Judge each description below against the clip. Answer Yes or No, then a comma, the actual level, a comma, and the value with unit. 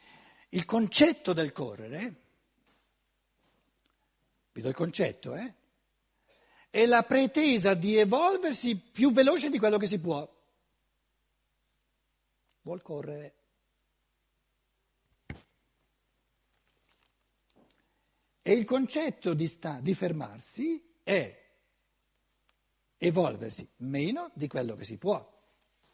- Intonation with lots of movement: Yes, wide, 8.5 semitones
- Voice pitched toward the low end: No, high, 190 Hz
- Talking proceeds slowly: Yes, slow, 90 wpm